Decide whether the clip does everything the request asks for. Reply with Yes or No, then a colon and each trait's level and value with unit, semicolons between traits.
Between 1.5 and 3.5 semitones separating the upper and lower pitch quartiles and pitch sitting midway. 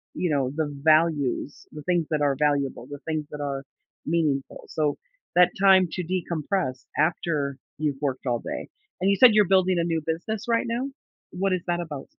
No: average, 4.0 semitones; medium, 160 Hz